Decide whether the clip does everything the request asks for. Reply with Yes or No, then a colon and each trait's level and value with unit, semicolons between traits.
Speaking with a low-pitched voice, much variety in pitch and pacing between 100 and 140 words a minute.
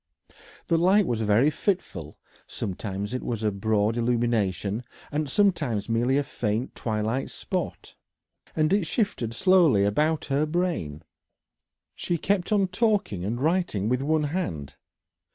Yes: low, 125 Hz; wide, 8.1 semitones; slow, 135 wpm